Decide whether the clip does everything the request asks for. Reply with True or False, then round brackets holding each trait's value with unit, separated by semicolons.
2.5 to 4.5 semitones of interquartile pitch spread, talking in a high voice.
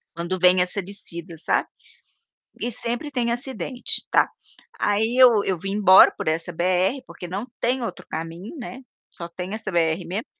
False (5.2 semitones; 195 Hz)